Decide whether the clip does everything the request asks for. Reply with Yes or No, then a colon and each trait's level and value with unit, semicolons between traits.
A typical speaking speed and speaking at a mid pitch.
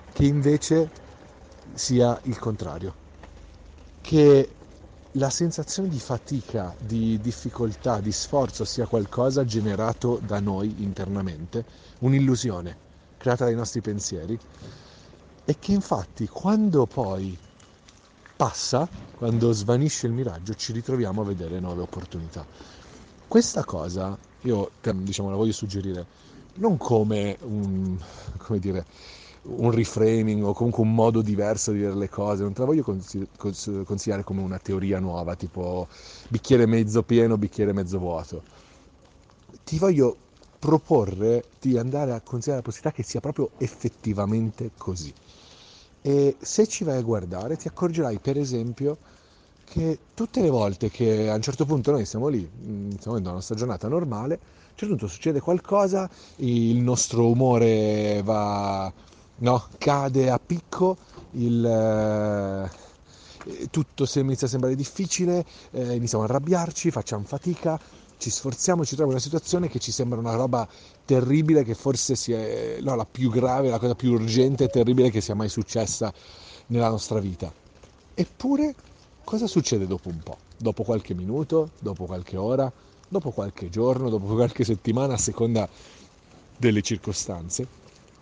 No: average, 135 wpm; low, 115 Hz